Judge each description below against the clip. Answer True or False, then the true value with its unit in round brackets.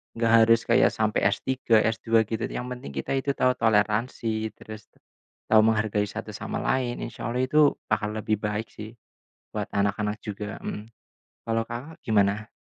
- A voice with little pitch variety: True (2.0 semitones)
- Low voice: True (110 Hz)